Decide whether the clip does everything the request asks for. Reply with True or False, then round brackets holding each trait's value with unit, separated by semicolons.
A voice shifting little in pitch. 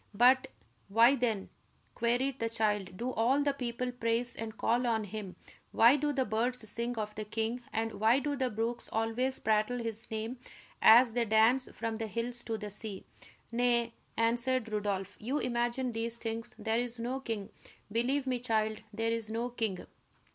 True (2.0 semitones)